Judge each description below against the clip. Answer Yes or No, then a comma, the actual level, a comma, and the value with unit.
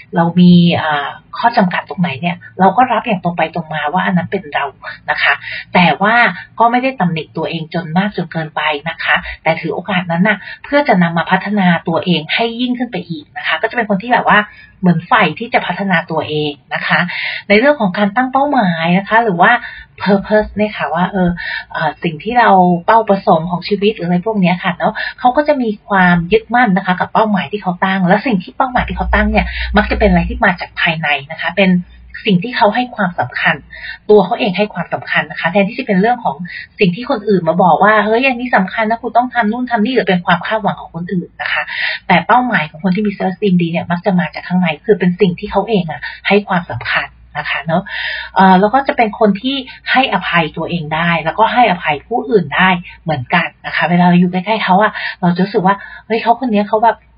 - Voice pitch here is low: No, high, 195 Hz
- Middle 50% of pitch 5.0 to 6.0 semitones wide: No, average, 4.2 semitones